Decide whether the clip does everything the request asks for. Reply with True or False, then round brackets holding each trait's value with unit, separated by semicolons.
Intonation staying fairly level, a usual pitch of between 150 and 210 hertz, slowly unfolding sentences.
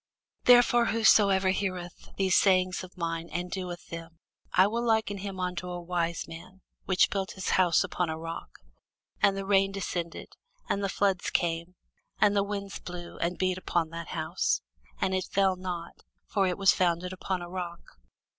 False (2.1 semitones; 185 Hz; 175 wpm)